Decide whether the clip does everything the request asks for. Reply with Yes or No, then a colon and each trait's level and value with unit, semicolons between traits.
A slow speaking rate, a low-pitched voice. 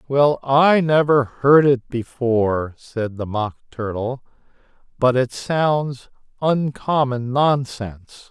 Yes: slow, 110 wpm; low, 130 Hz